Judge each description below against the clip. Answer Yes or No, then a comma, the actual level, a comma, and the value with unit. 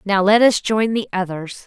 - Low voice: No, high, 200 Hz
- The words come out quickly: Yes, fast, 215 wpm